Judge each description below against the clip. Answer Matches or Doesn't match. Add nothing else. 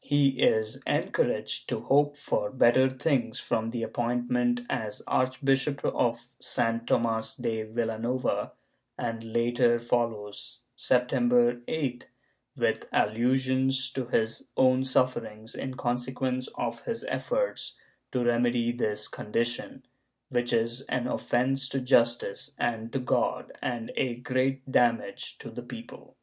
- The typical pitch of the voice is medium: Doesn't match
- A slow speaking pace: Matches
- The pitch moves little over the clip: Matches